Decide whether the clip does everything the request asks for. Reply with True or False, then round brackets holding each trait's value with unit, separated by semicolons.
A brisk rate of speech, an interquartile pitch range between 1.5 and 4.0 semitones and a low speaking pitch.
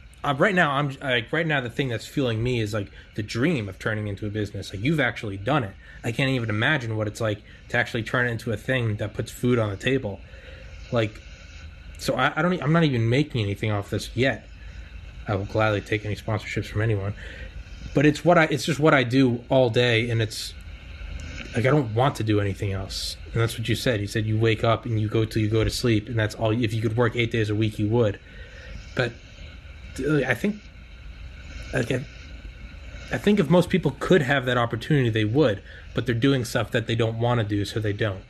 False (230 wpm; 4.6 semitones; 110 Hz)